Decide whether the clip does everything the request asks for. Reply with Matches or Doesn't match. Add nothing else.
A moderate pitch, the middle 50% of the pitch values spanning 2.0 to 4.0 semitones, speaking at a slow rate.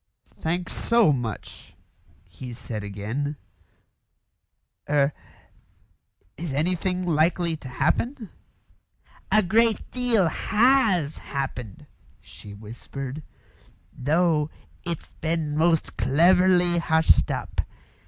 Doesn't match